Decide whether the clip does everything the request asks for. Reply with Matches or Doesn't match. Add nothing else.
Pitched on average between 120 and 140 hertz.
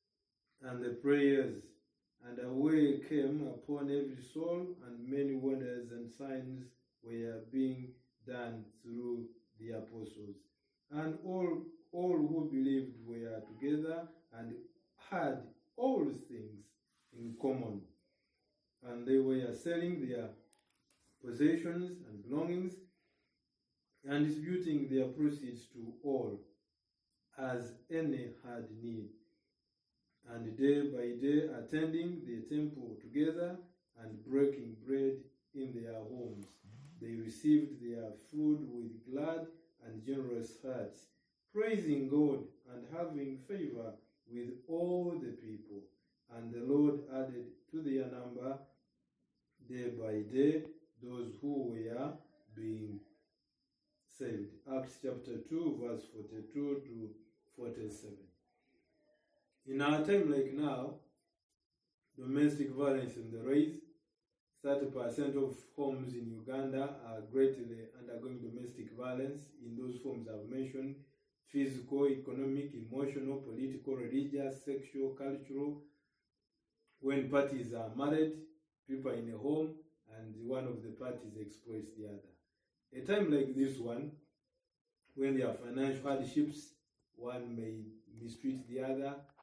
Matches